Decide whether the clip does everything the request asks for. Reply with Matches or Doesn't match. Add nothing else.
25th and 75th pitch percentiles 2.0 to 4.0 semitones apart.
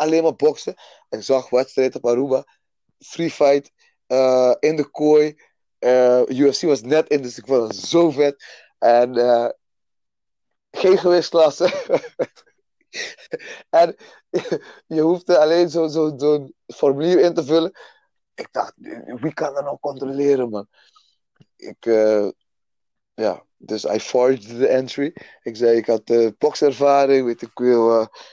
Doesn't match